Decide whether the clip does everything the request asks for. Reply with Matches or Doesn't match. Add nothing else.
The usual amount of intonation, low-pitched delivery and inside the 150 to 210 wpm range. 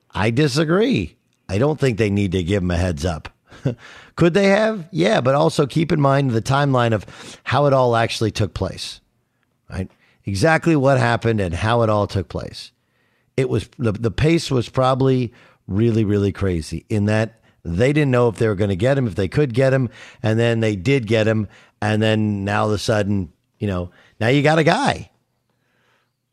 Matches